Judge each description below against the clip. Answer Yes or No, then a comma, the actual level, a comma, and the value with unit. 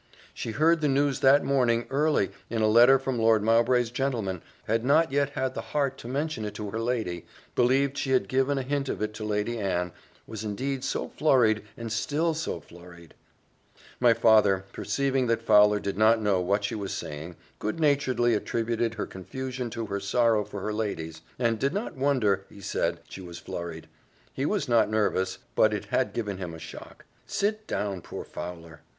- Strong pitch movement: No, average, 4.7 semitones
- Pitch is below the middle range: Yes, low, 115 Hz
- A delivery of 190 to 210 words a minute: Yes, average, 195 wpm